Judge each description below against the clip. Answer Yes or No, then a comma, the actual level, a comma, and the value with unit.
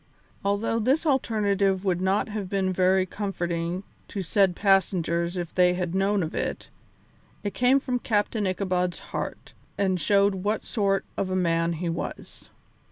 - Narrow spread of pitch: Yes, narrow, 2.3 semitones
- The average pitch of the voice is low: No, high, 190 Hz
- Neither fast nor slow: Yes, average, 155 wpm